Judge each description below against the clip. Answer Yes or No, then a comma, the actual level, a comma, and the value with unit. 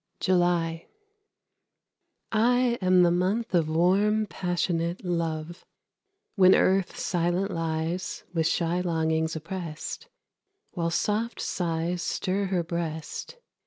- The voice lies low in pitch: No, medium, 175 Hz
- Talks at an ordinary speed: No, slow, 100 wpm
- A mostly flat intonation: Yes, narrow, 2.3 semitones